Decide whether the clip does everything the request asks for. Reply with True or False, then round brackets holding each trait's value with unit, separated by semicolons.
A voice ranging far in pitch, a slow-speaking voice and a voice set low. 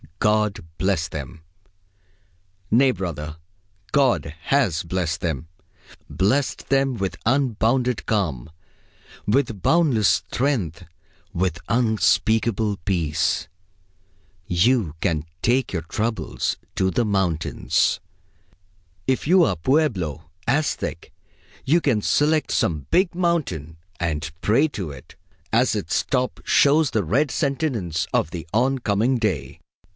True (7.9 semitones; 110 wpm; 105 Hz)